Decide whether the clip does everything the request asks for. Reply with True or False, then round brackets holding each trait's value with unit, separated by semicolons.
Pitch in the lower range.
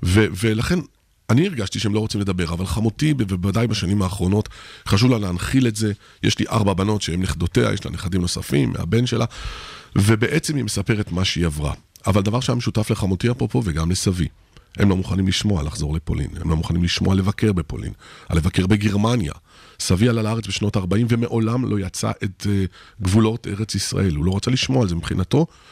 True (100 Hz)